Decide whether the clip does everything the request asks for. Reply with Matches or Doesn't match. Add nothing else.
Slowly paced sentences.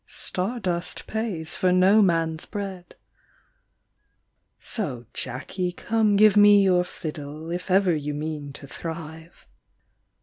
Matches